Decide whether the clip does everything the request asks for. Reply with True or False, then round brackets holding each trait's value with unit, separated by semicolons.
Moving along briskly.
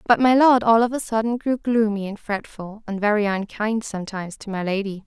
True (215 wpm)